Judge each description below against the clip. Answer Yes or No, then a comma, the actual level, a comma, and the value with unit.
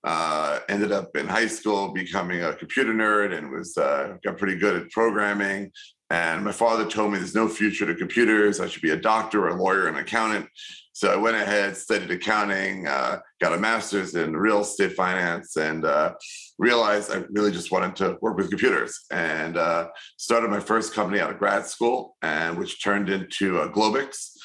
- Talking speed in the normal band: Yes, average, 195 wpm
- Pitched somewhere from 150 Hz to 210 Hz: No, low, 100 Hz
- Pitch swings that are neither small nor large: No, narrow, 2.3 semitones